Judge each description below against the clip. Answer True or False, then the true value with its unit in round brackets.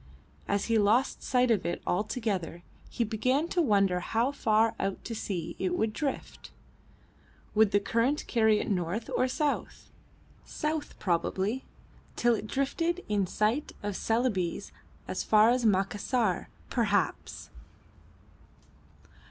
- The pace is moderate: False (125 wpm)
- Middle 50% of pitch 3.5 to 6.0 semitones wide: True (4.1 semitones)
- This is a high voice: True (220 Hz)